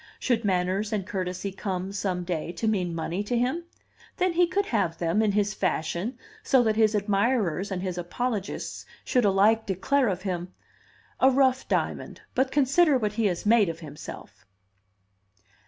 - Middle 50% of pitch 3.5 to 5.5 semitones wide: Yes, average, 4.9 semitones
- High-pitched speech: Yes, high, 205 Hz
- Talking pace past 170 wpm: No, average, 165 wpm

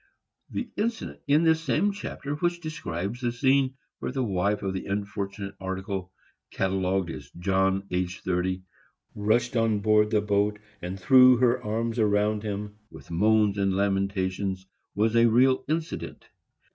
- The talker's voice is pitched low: Yes, low, 105 Hz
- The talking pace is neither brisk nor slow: Yes, average, 145 wpm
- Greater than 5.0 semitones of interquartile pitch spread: No, average, 4.2 semitones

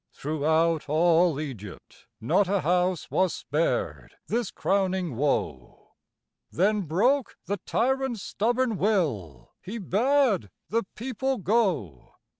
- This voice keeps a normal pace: No, slow, 105 wpm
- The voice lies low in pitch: No, medium, 185 Hz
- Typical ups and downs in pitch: No, wide, 6.4 semitones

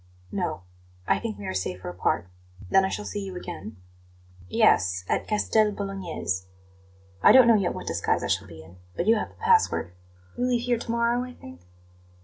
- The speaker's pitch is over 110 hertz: Yes, medium, 185 Hz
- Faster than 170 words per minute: Yes, average, 190 wpm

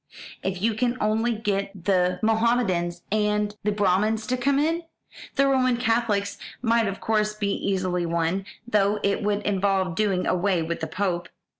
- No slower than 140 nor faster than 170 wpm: Yes, average, 160 wpm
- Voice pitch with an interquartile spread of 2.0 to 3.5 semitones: Yes, average, 3.1 semitones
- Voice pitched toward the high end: Yes, high, 205 Hz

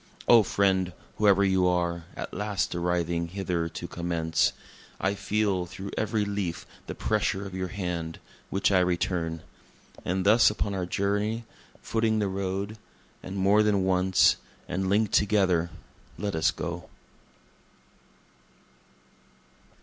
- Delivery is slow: Yes, slow, 125 wpm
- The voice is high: No, very low, 95 Hz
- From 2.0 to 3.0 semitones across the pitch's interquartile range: Yes, narrow, 2.5 semitones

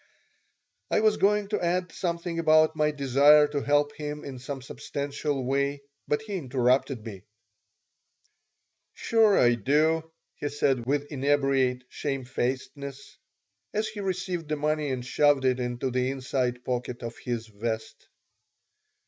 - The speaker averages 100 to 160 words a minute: Yes, slow, 135 wpm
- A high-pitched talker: No, medium, 140 Hz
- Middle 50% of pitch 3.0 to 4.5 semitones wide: Yes, average, 3.6 semitones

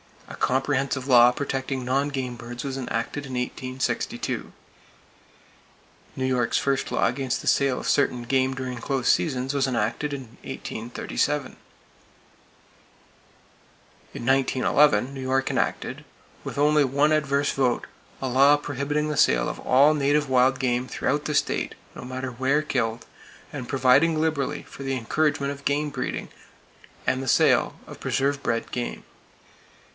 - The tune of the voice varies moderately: No, narrow, 2.0 semitones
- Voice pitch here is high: No, low, 135 Hz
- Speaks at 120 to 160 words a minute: Yes, average, 140 wpm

